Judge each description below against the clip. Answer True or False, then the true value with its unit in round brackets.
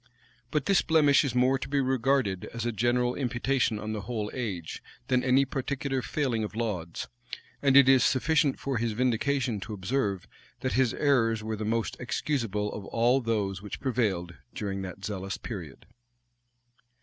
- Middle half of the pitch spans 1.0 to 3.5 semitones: False (4.1 semitones)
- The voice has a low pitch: True (120 Hz)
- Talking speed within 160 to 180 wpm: True (165 wpm)